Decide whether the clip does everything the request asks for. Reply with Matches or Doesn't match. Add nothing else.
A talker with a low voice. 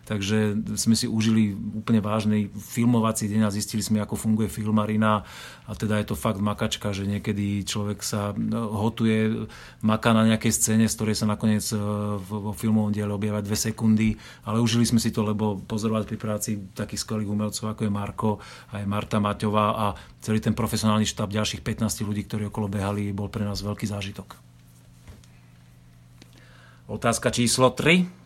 Matches